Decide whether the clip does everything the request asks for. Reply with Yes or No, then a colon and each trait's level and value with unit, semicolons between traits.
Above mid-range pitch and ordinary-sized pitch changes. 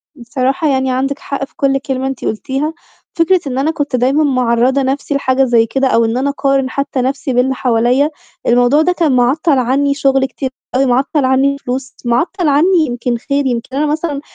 No: very high, 270 Hz; narrow, 2.0 semitones